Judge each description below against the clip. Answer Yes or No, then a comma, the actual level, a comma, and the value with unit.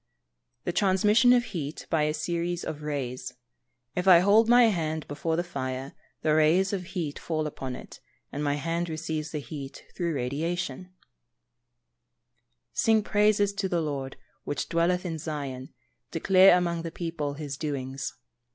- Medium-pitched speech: Yes, medium, 165 Hz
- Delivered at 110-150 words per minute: No, average, 160 wpm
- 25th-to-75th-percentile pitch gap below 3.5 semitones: No, average, 3.8 semitones